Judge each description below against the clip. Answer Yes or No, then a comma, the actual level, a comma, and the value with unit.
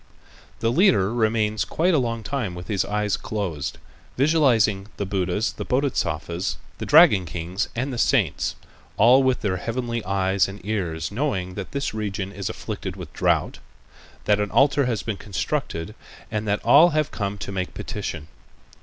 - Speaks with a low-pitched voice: Yes, low, 105 Hz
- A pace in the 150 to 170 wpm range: Yes, average, 165 wpm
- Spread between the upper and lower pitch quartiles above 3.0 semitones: Yes, average, 4.6 semitones